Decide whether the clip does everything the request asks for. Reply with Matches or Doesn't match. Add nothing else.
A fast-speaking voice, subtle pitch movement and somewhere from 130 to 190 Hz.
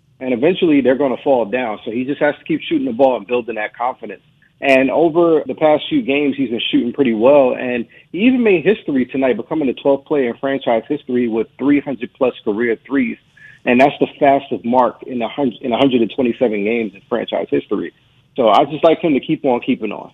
Doesn't match